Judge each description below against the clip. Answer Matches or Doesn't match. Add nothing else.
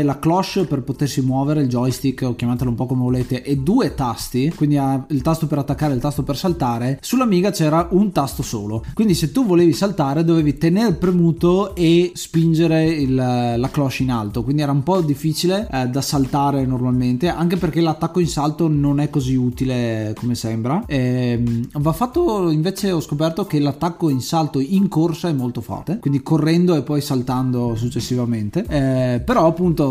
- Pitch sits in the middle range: Matches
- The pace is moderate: Doesn't match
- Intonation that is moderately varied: Matches